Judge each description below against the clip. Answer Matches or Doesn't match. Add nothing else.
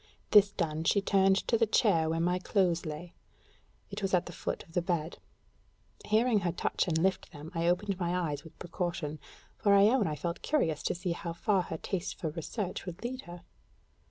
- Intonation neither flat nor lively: Matches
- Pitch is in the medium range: Matches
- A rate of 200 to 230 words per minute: Matches